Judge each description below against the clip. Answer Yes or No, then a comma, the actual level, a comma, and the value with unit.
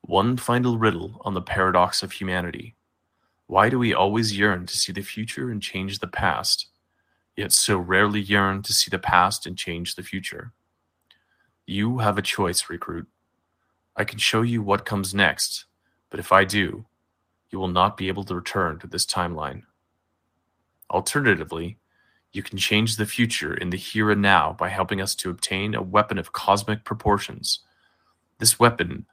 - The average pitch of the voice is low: Yes, low, 100 Hz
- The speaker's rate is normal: Yes, average, 170 wpm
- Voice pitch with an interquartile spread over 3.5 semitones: No, average, 3.2 semitones